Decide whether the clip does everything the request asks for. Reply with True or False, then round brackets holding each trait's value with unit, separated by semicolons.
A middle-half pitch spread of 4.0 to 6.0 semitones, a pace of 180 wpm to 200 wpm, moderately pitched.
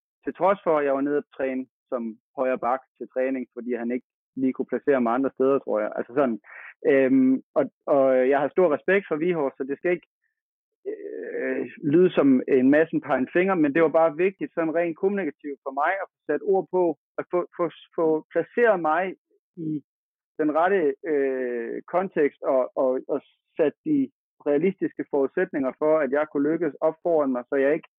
True (5.3 semitones; 195 wpm; 155 Hz)